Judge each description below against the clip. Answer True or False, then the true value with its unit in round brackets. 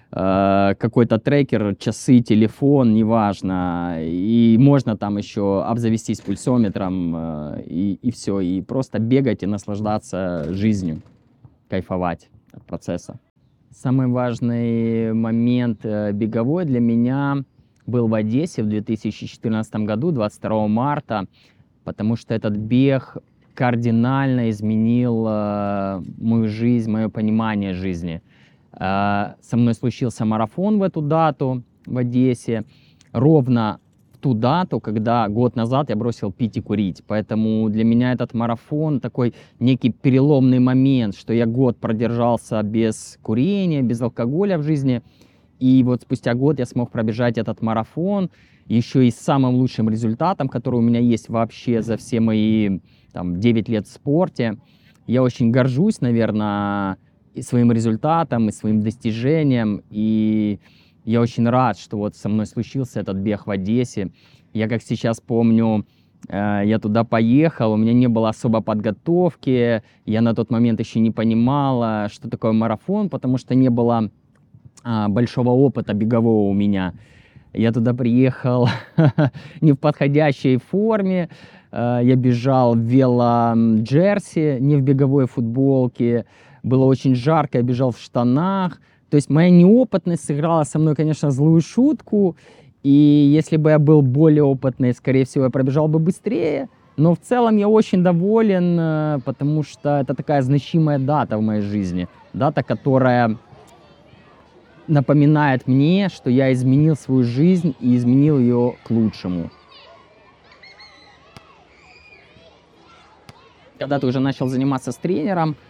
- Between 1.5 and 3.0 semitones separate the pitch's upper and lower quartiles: False (4.0 semitones)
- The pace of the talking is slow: False (130 wpm)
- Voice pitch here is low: True (120 Hz)